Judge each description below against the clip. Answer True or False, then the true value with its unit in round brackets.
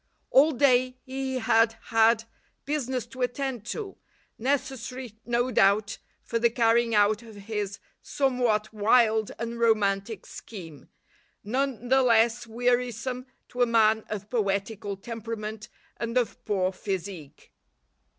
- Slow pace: True (120 wpm)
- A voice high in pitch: True (230 Hz)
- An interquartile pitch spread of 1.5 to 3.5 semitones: True (2.9 semitones)